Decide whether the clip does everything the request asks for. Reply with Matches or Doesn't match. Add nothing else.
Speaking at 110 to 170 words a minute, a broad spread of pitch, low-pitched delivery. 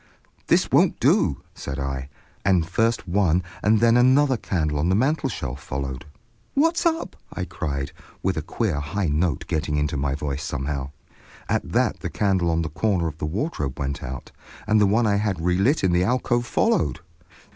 Doesn't match